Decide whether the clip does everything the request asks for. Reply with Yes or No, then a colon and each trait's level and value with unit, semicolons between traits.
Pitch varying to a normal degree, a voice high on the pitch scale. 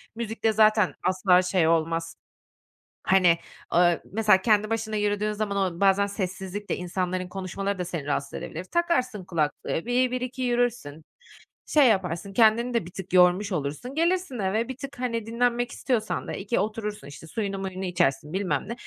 Yes: average, 4.3 semitones; high, 200 Hz